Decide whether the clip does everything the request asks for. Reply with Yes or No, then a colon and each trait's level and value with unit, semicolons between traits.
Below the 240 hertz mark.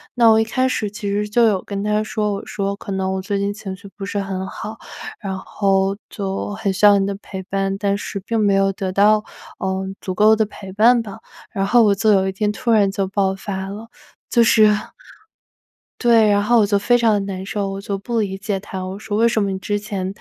Yes: high, 200 Hz